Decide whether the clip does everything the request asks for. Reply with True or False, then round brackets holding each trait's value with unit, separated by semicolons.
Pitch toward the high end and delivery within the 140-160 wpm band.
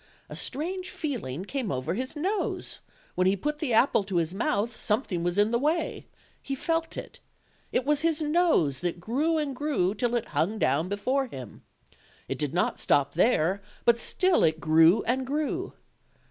False (235 Hz; 175 wpm)